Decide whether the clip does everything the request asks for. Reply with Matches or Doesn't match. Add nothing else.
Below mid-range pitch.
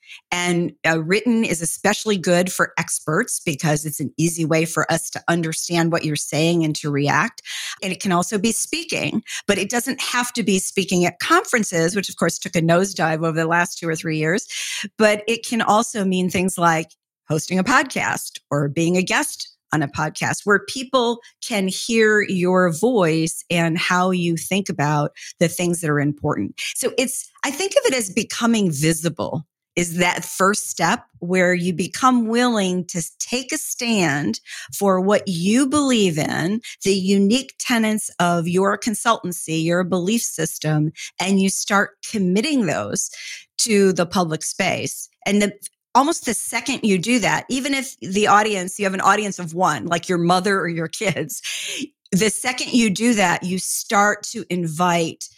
Doesn't match